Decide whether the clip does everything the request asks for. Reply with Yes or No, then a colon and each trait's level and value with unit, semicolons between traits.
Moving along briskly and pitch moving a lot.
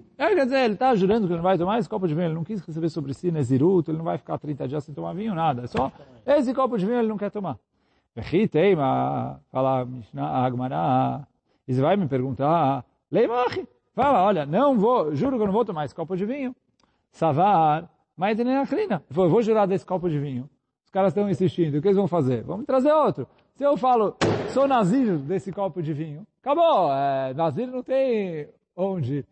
Yes: fast, 205 wpm; wide, 7.5 semitones